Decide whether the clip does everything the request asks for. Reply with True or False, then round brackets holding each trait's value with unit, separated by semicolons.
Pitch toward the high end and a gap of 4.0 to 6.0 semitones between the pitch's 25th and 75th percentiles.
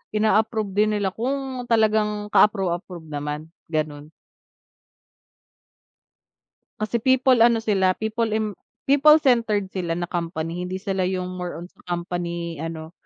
True (195 Hz; 4.3 semitones)